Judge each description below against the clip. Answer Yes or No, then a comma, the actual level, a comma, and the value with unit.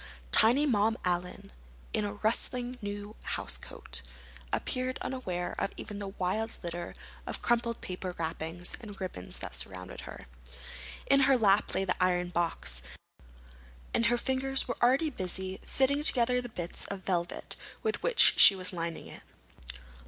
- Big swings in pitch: Yes, wide, 5.8 semitones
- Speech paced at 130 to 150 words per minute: Yes, average, 145 wpm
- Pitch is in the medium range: No, high, 205 Hz